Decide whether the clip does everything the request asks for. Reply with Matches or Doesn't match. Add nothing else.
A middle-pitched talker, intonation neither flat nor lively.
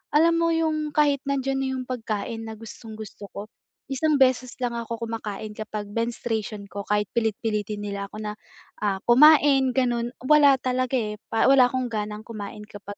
Doesn't match